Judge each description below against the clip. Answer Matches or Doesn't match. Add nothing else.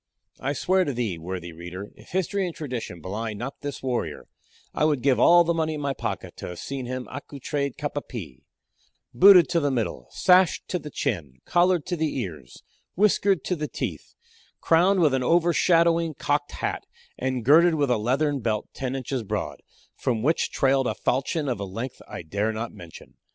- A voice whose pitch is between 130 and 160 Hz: Matches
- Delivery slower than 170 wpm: Doesn't match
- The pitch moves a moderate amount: Doesn't match